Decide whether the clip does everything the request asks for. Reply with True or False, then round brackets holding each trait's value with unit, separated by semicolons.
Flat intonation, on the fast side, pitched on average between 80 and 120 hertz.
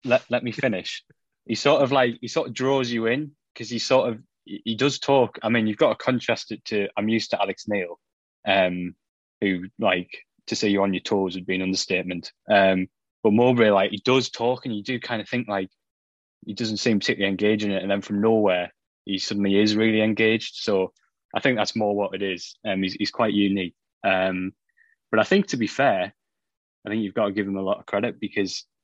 False (3.6 semitones; 230 wpm; 105 Hz)